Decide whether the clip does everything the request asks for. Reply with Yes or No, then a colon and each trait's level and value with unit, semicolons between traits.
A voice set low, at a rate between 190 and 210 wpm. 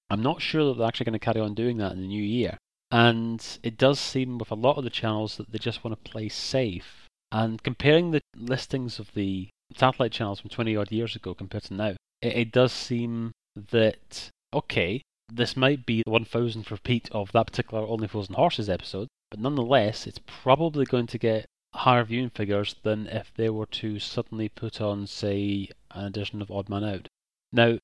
Yes: low, 115 Hz; average, 200 wpm